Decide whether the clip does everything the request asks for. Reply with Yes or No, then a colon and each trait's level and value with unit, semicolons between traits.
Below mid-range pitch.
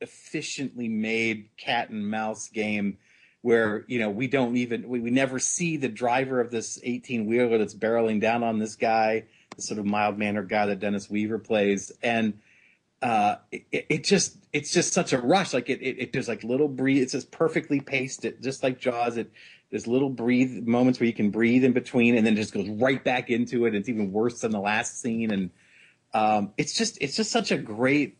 Yes: low, 120 Hz